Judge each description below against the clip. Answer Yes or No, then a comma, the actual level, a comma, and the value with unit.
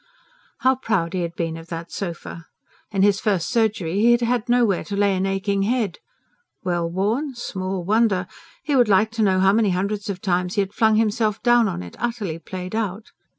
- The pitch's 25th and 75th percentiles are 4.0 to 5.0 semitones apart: No, average, 3.5 semitones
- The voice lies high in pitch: Yes, high, 200 Hz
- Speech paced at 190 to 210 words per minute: Yes, average, 200 wpm